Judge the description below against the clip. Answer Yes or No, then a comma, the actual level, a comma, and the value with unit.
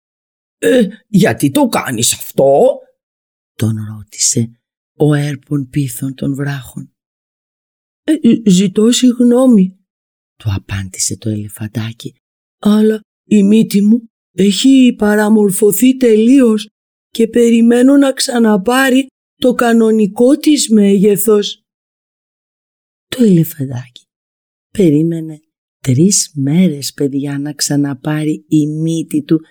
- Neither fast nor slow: No, slow, 90 wpm